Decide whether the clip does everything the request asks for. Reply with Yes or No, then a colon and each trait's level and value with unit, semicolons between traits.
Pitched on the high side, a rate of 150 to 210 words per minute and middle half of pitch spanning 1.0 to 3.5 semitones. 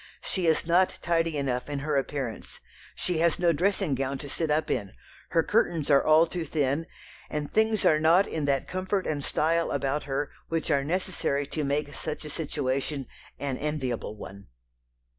No: medium, 150 Hz; average, 180 wpm; average, 3.2 semitones